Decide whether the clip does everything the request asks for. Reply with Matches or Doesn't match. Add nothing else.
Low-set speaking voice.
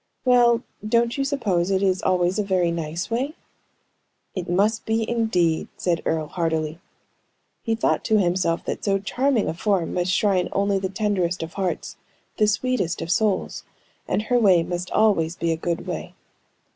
Doesn't match